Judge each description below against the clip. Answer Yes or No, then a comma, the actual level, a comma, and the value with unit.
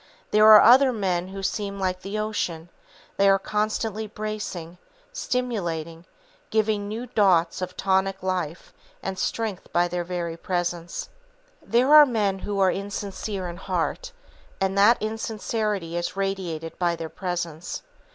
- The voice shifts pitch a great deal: No, average, 3.4 semitones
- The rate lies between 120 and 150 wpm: Yes, average, 140 wpm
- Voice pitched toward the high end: Yes, high, 195 Hz